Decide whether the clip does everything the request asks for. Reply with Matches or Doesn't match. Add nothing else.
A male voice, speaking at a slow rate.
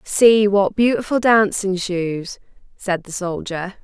Doesn't match